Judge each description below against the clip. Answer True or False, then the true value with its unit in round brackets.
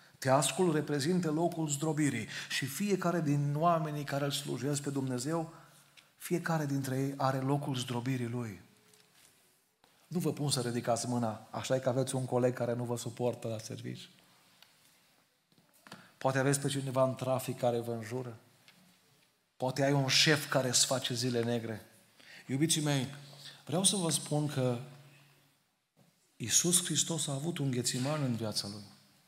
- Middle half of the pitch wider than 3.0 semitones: True (3.6 semitones)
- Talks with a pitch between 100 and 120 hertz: False (135 Hz)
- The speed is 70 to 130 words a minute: False (145 wpm)